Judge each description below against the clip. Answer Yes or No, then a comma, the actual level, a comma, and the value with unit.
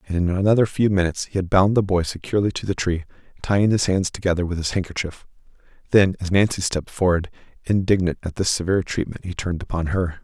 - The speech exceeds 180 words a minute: Yes, fast, 205 wpm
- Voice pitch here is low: Yes, very low, 90 Hz